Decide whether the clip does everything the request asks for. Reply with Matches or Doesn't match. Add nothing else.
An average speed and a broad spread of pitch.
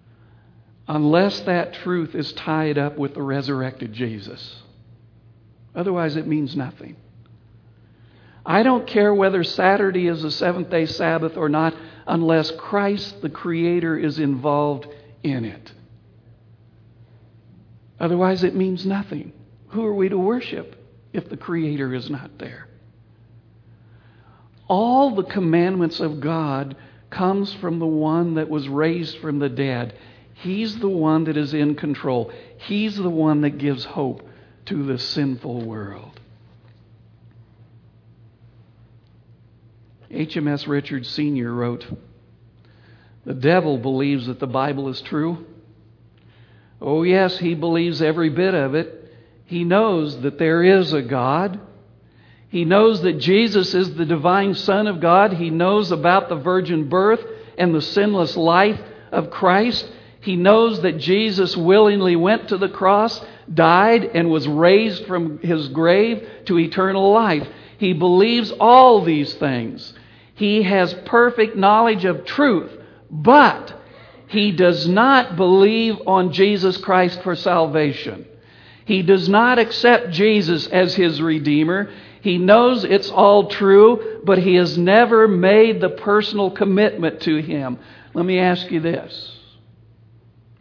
Doesn't match